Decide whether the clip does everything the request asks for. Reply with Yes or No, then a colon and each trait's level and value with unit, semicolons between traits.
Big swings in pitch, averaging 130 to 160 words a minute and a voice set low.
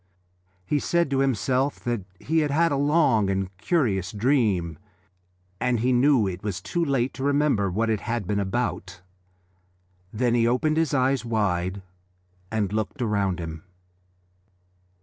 Yes: wide, 5.8 semitones; average, 150 wpm; low, 115 Hz